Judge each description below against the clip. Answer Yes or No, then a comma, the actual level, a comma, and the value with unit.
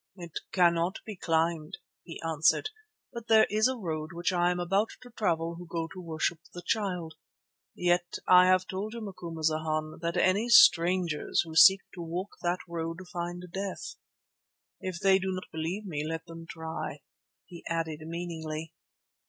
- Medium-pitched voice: Yes, medium, 175 Hz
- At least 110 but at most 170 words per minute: Yes, average, 160 wpm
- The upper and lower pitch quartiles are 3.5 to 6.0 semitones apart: No, narrow, 2.4 semitones